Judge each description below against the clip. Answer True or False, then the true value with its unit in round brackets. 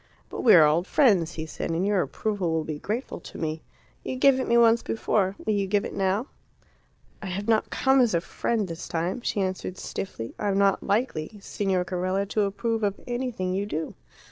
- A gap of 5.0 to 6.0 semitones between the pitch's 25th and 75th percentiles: False (3.8 semitones)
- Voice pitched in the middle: False (195 Hz)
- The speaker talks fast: True (210 wpm)